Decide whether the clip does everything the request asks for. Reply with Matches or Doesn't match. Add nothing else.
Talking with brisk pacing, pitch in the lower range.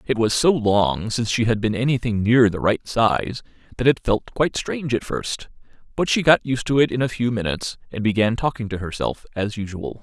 Matches